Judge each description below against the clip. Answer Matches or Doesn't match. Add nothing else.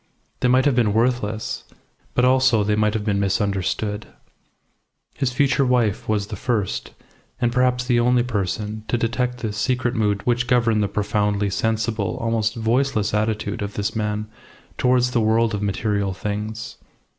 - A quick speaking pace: Doesn't match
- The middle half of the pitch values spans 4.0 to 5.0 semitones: Doesn't match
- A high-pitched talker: Doesn't match